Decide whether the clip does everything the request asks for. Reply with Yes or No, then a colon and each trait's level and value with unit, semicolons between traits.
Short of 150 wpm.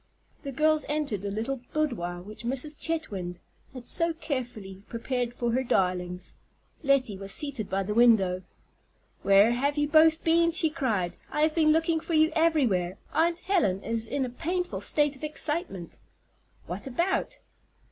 No: average, 155 wpm